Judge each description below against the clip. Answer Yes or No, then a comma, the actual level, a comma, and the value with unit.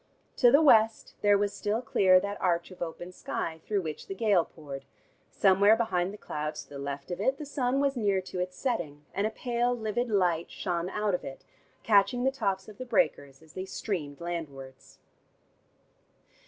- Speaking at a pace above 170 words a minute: Yes, average, 190 wpm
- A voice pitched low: No, high, 195 Hz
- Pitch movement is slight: No, average, 4.8 semitones